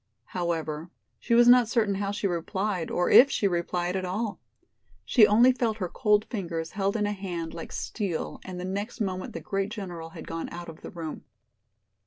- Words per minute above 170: Yes, average, 195 wpm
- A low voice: No, high, 190 Hz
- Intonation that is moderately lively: Yes, average, 3.4 semitones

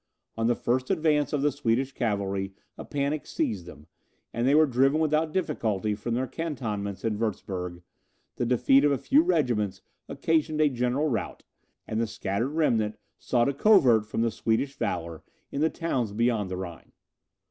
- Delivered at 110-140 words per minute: No, average, 170 wpm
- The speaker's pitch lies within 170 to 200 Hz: No, low, 120 Hz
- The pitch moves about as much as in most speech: No, wide, 5.7 semitones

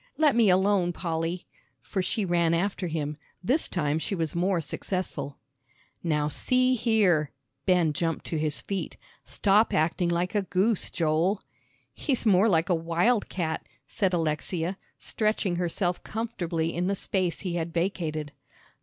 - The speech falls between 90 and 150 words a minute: Yes, average, 145 wpm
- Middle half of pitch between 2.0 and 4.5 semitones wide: Yes, average, 3.3 semitones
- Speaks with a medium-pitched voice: Yes, medium, 175 Hz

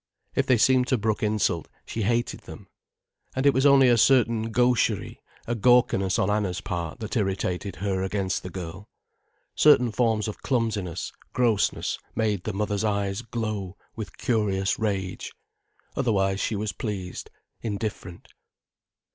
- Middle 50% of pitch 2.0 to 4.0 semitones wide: Yes, average, 3.3 semitones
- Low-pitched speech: Yes, low, 105 Hz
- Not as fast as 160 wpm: Yes, average, 140 wpm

